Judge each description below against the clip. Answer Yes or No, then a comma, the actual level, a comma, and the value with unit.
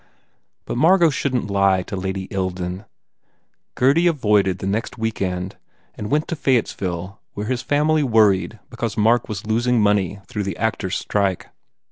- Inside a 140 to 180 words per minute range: Yes, average, 155 wpm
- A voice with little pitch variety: No, average, 4.3 semitones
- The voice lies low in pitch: Yes, low, 105 Hz